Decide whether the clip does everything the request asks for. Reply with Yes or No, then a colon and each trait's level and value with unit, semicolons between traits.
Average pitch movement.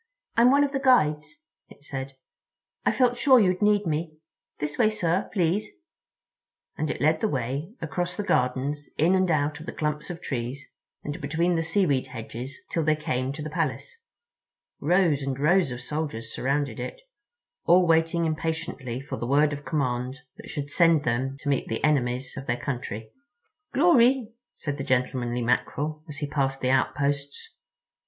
Yes: average, 4.2 semitones